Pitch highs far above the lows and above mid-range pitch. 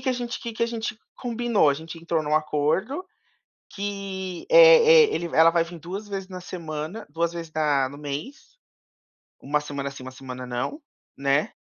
No: wide, 6.8 semitones; medium, 170 Hz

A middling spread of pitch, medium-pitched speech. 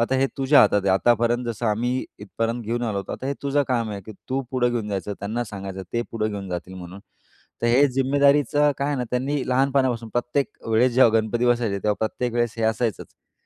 No: average, 3.4 semitones; low, 120 Hz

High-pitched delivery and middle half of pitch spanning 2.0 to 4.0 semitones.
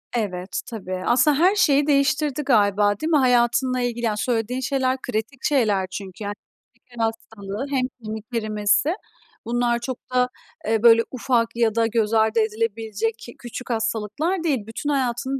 Yes: high, 235 Hz; average, 3.2 semitones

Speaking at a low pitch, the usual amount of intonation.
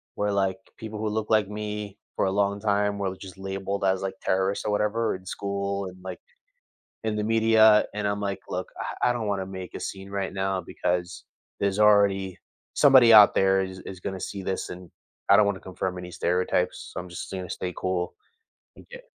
No: low, 100 Hz; narrow, 1.9 semitones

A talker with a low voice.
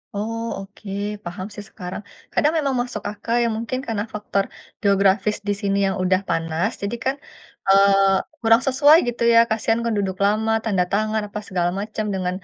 No: high, 210 Hz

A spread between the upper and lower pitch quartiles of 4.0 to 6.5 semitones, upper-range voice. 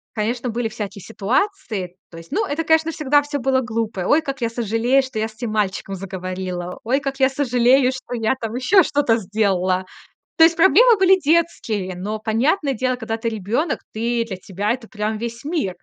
Yes: average, 4.6 semitones; high, 235 Hz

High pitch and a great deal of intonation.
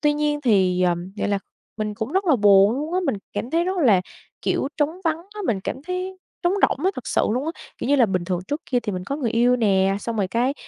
Yes: high, 245 Hz; wide, 7.1 semitones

